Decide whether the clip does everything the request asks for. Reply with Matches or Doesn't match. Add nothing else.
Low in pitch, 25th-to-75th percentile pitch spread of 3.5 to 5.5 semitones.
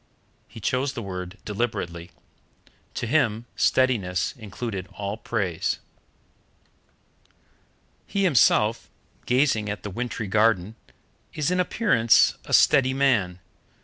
Matches